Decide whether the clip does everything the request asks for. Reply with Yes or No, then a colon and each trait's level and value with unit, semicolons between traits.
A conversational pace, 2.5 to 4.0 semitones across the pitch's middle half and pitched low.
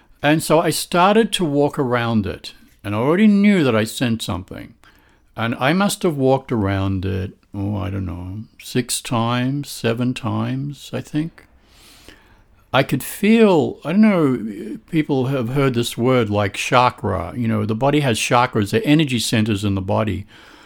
No: average, 170 wpm; average, 5.1 semitones; low, 125 Hz